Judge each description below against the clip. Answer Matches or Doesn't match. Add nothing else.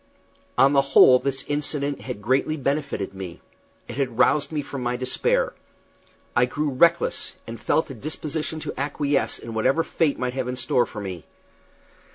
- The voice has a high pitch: Doesn't match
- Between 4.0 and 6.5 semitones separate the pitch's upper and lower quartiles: Doesn't match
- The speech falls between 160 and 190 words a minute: Matches